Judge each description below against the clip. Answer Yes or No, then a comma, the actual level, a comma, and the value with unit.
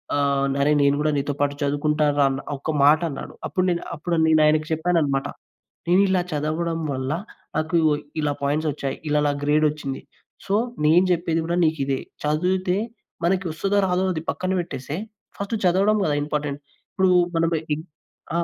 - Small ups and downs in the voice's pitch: No, average, 3.3 semitones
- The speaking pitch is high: No, medium, 155 Hz